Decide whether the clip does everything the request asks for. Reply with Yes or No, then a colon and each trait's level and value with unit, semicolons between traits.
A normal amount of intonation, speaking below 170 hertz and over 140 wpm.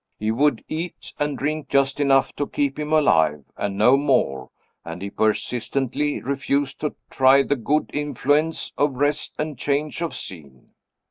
Yes: average, 4.3 semitones; medium, 140 Hz; average, 155 wpm